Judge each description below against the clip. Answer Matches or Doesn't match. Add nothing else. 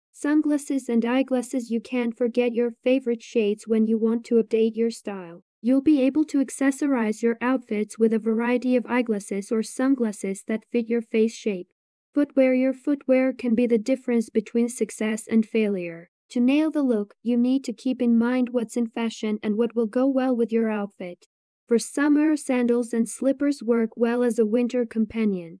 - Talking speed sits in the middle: Matches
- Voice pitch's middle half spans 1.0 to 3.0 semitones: Matches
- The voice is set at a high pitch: Matches